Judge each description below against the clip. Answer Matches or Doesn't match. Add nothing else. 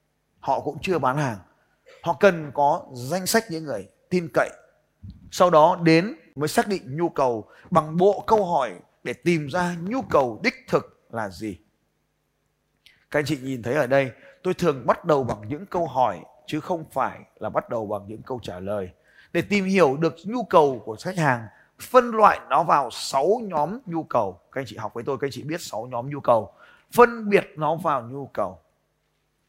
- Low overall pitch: Doesn't match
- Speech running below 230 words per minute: Matches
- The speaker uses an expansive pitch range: Matches